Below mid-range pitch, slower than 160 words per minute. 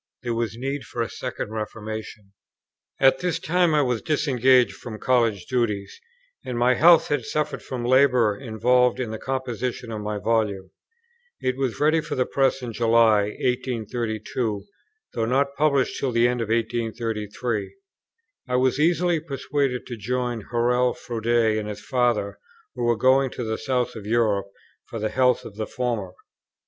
No: low, 120 Hz; average, 165 wpm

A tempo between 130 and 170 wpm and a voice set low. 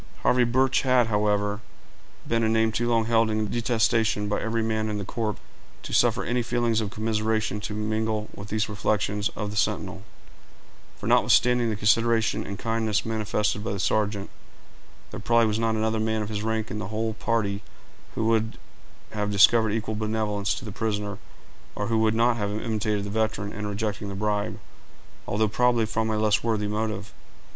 No: average, 180 wpm; low, 110 Hz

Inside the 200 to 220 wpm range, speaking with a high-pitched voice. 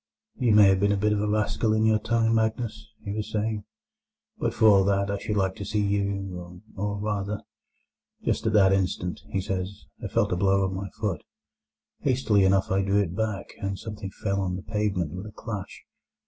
No: fast, 205 wpm; low, 100 Hz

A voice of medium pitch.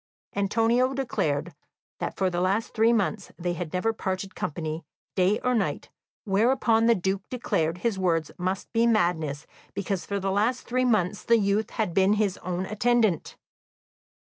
No: high, 200 Hz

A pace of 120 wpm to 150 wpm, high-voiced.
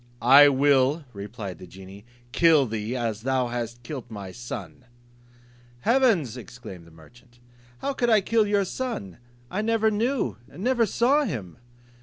No: average, 145 wpm; low, 130 Hz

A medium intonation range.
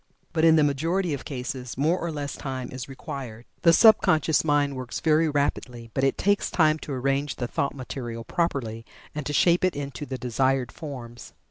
Yes: average, 3.7 semitones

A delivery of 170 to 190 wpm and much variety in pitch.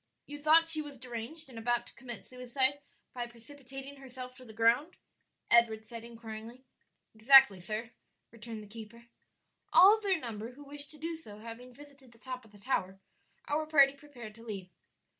No: average, 180 wpm; average, 3.8 semitones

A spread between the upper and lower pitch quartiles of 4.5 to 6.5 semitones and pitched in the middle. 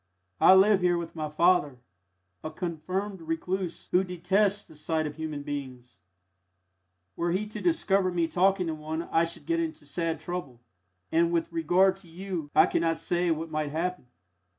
No: average, 2.9 semitones; medium, 170 Hz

